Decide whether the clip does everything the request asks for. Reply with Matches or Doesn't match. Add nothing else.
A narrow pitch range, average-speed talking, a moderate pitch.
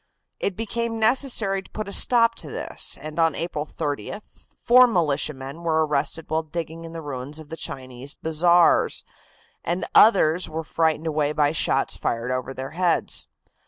Doesn't match